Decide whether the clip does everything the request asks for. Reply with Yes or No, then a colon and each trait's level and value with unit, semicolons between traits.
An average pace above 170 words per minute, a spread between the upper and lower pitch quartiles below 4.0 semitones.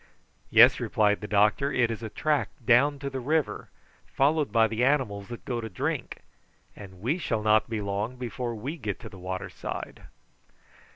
No: average, 180 wpm; average, 4.3 semitones